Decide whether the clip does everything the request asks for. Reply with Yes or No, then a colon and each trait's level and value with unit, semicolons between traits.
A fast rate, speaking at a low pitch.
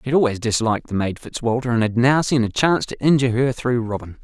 Yes: fast, 255 wpm; low, 120 Hz